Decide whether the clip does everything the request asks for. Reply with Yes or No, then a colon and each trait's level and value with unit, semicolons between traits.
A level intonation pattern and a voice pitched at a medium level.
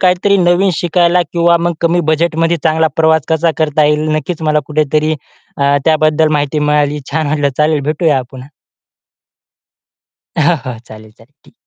Yes: narrow, 2.3 semitones; medium, 155 Hz